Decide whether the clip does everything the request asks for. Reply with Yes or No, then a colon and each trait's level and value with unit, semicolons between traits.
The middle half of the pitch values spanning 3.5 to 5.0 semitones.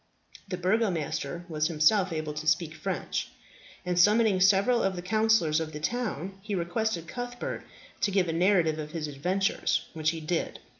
Yes: average, 4.4 semitones